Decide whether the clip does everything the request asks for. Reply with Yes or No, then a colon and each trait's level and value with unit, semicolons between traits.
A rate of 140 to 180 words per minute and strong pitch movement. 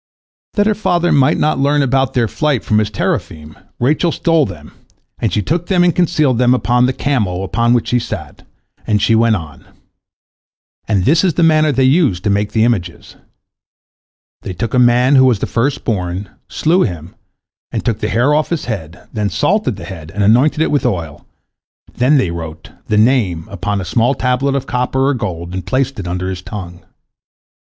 No: average, 195 wpm; wide, 6.6 semitones